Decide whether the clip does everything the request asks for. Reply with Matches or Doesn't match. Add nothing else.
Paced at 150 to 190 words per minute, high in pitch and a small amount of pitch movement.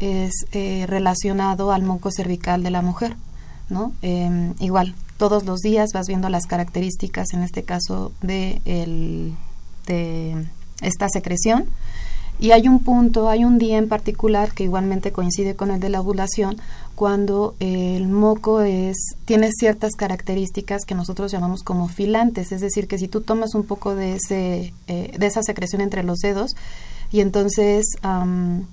Matches